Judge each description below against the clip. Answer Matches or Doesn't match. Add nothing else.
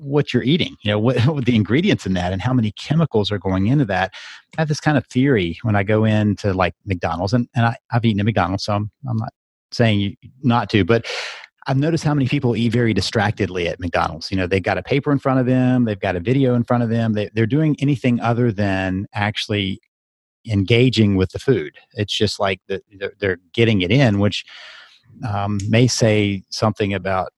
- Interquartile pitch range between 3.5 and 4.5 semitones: Matches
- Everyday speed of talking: Doesn't match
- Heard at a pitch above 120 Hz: Doesn't match